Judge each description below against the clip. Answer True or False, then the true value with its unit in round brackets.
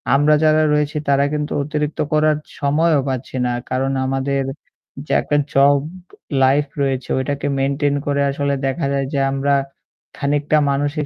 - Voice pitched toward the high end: False (140 Hz)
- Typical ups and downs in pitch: False (1.4 semitones)